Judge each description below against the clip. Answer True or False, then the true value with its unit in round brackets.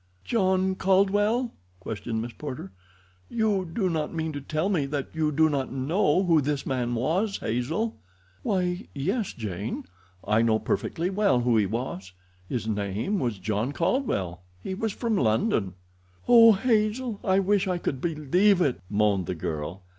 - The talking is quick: False (155 wpm)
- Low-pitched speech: False (155 Hz)